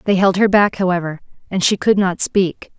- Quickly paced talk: Yes, fast, 215 wpm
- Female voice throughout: Yes, female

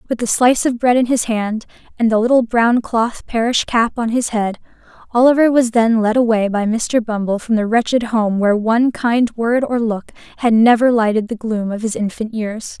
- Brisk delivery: Yes, fast, 210 wpm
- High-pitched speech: Yes, high, 230 Hz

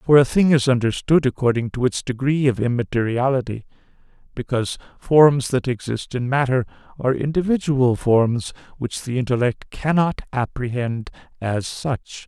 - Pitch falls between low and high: No, low, 130 Hz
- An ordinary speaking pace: No, slow, 130 wpm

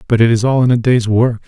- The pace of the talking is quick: Yes, fast, 325 wpm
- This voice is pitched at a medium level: No, low, 120 Hz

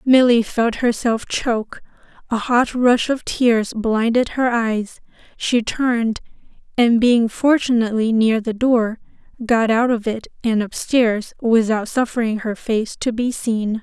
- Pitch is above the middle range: Yes, high, 230 Hz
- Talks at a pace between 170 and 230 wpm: No, average, 145 wpm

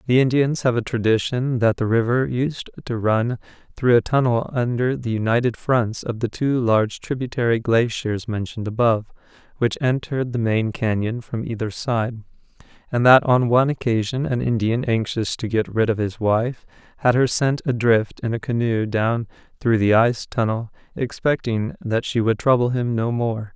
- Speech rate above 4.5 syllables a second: Yes, 4.9 syllables/s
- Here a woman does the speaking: No, male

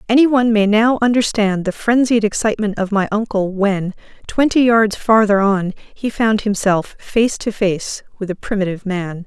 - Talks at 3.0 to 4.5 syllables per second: No, 4.9 syllables/s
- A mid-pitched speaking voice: No, high, 210 Hz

